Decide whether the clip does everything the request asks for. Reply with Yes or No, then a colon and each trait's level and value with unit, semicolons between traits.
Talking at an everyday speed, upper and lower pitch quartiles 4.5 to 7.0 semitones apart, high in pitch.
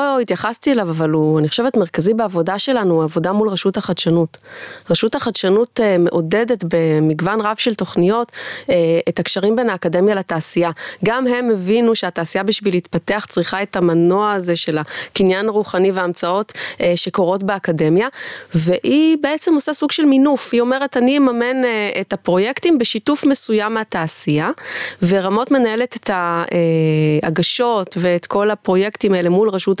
Yes: average, 135 wpm; average, 5.0 semitones; high, 195 Hz